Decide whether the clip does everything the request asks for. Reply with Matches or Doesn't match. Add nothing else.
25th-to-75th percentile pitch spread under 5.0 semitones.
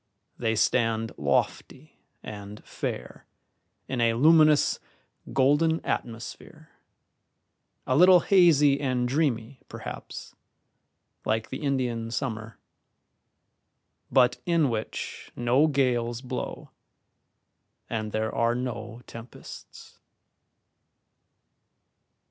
Matches